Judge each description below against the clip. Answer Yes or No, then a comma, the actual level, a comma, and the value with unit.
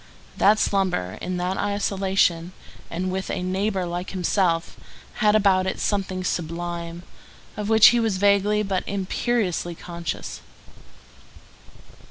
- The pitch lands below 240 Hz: Yes, high, 190 Hz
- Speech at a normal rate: No, slow, 120 wpm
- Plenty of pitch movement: No, narrow, 2.4 semitones